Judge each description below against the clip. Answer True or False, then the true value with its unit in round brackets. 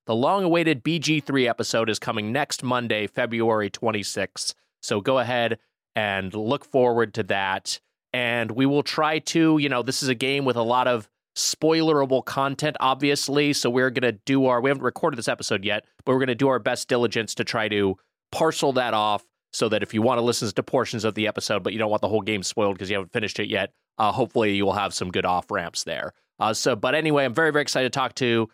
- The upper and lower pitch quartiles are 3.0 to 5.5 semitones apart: True (4.0 semitones)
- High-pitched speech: False (125 Hz)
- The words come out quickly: True (225 wpm)